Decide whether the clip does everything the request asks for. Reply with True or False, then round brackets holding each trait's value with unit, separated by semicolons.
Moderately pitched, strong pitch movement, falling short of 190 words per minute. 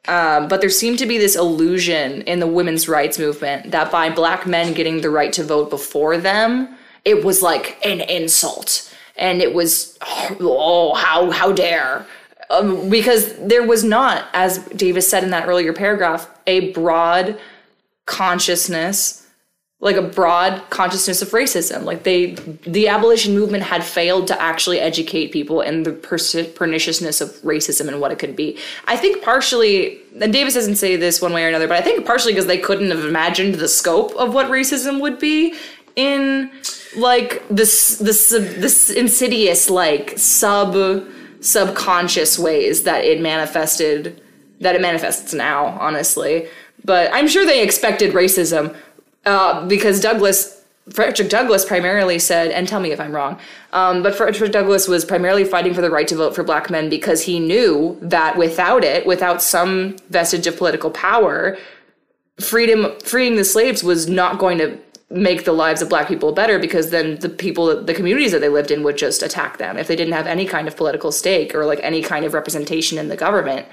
False (180 Hz; 4.1 semitones; 175 wpm)